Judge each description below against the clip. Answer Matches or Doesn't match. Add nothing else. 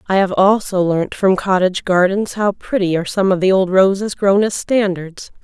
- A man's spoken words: Doesn't match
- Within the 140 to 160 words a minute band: Doesn't match